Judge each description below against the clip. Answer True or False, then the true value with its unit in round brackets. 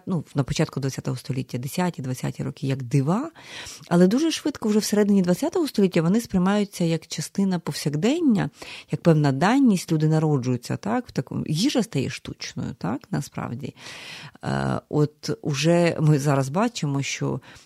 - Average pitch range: False (6.4 semitones)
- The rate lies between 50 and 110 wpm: False (140 wpm)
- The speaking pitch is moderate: True (165 Hz)